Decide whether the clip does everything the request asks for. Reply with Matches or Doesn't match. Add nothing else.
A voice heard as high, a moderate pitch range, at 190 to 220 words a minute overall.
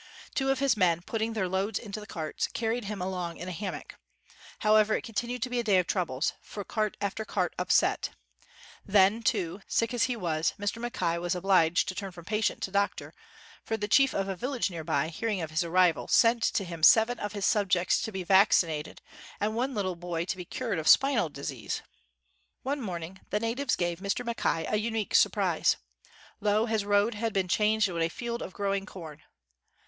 Matches